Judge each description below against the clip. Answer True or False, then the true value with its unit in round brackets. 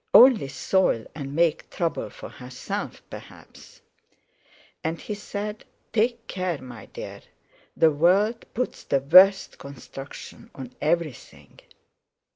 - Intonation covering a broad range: True (6.7 semitones)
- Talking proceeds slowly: True (110 wpm)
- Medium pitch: True (170 Hz)